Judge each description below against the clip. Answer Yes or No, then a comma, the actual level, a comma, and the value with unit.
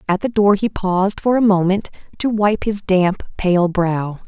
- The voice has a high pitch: Yes, high, 195 Hz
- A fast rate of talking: No, average, 195 wpm